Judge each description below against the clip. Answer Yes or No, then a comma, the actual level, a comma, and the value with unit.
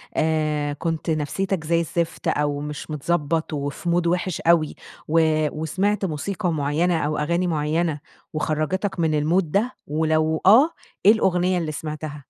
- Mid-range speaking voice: Yes, medium, 160 Hz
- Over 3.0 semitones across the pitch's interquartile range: No, average, 2.7 semitones